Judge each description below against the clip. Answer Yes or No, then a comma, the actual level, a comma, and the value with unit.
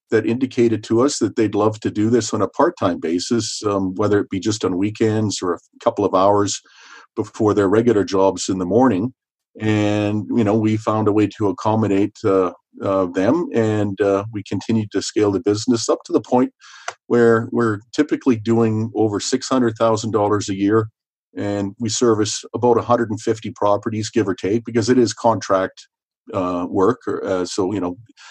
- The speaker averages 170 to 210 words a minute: Yes, average, 195 wpm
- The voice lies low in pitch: Yes, low, 110 Hz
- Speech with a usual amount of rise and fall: No, narrow, 2.1 semitones